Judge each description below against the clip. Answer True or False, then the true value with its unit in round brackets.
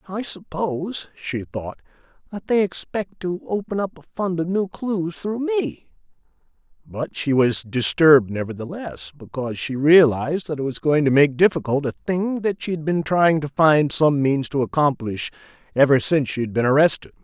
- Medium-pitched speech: True (155 Hz)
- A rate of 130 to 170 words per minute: False (180 wpm)